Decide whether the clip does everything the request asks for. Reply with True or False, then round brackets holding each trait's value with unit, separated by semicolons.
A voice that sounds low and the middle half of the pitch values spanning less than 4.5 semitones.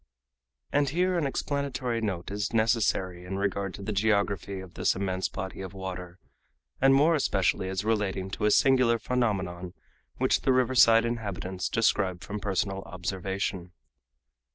True (100 Hz; 3.8 semitones)